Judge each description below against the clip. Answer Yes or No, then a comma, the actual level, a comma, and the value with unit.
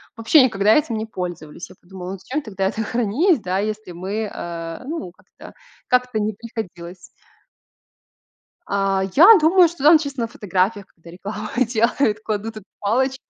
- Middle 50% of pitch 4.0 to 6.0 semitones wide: Yes, average, 4.7 semitones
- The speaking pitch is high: Yes, high, 215 Hz